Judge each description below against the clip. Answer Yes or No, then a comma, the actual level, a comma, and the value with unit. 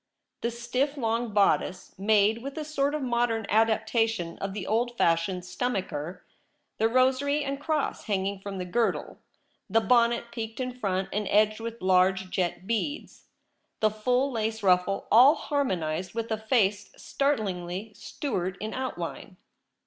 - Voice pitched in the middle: No, high, 220 Hz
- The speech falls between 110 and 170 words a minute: Yes, average, 150 wpm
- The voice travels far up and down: No, average, 4.5 semitones